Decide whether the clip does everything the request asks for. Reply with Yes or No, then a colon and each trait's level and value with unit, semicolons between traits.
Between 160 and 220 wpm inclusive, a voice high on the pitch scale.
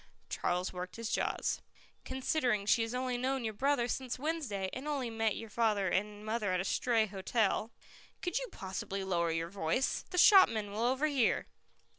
Yes: average, 175 wpm; high, 225 Hz